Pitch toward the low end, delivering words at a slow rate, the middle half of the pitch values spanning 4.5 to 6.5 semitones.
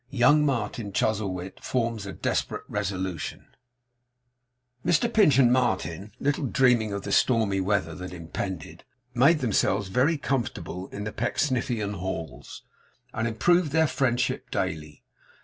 Yes: low, 110 Hz; slow, 125 wpm; wide, 5.4 semitones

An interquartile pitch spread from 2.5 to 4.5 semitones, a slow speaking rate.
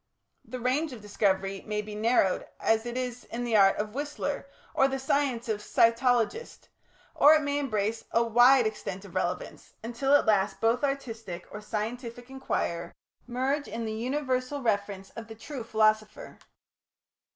No: average, 3.8 semitones; average, 165 wpm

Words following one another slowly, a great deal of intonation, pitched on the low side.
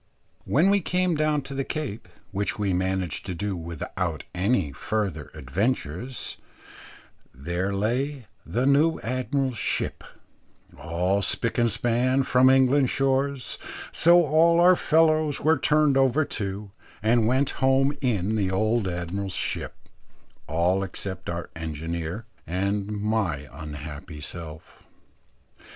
Yes: slow, 125 wpm; wide, 7.1 semitones; low, 110 Hz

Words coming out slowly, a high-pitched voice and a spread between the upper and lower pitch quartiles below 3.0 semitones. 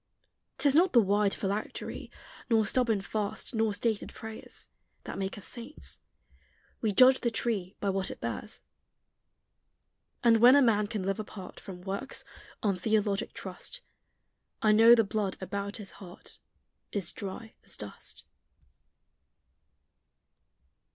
Yes: slow, 130 wpm; high, 210 Hz; narrow, 2.6 semitones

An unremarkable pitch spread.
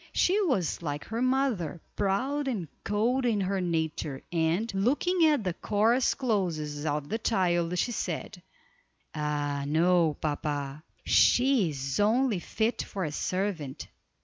No: wide, 7.2 semitones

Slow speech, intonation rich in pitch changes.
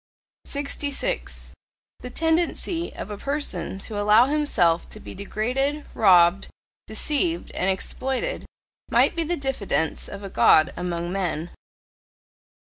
Yes: slow, 115 wpm; wide, 7.7 semitones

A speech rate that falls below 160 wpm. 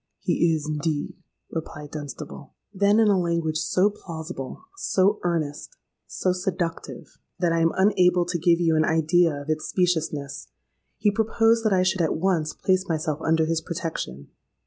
Yes: average, 150 wpm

